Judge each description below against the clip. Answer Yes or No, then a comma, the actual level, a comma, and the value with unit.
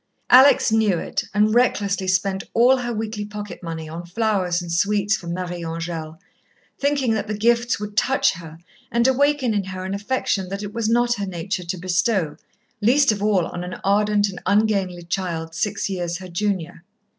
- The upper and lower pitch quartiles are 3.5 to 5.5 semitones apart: Yes, average, 3.8 semitones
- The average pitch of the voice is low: No, high, 200 Hz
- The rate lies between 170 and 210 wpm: Yes, average, 180 wpm